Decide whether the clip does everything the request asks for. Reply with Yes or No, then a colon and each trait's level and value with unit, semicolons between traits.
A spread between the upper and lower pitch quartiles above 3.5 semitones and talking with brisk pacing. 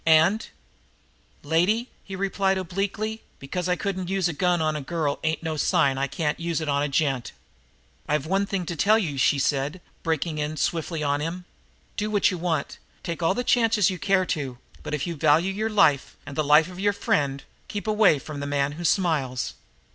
Yes: average, 4.6 semitones; fast, 210 wpm